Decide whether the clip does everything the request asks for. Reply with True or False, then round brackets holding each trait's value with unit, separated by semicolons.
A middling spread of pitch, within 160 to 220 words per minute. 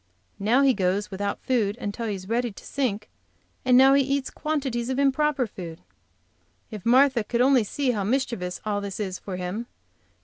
True (4.7 semitones; 180 wpm)